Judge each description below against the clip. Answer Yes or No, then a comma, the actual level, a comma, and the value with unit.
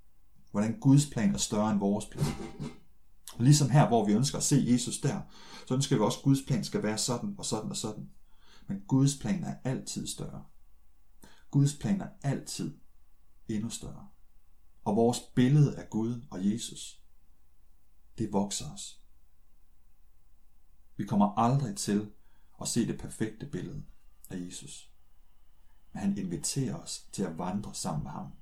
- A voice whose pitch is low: Yes, low, 105 Hz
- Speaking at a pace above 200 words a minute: No, average, 160 wpm